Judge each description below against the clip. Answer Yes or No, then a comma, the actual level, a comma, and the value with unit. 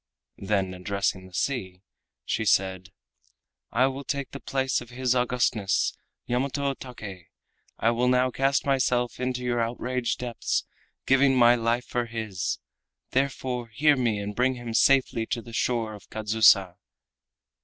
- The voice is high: No, low, 120 Hz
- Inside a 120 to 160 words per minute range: Yes, average, 145 wpm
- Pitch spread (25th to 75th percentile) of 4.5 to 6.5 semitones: No, average, 3.1 semitones